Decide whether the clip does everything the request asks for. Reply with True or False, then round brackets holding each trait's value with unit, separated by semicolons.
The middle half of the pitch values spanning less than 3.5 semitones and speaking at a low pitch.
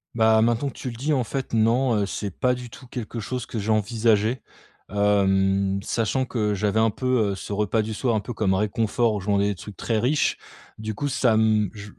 True (2.8 semitones; 110 Hz)